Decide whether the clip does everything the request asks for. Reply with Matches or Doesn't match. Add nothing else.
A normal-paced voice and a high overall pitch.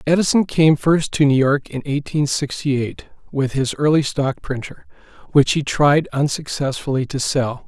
Doesn't match